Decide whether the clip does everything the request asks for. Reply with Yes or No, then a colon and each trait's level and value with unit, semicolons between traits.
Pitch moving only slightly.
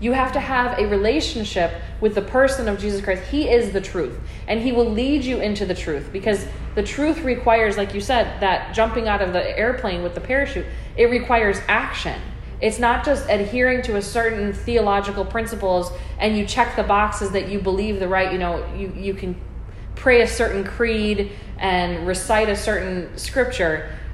No: average, 3.5 semitones